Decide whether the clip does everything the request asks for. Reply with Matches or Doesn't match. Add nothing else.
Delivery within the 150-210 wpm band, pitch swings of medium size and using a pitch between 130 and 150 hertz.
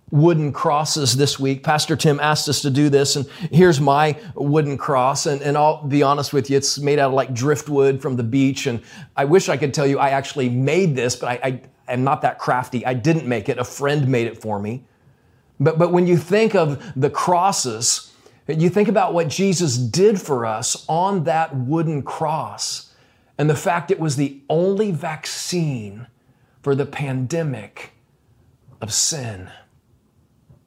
Matches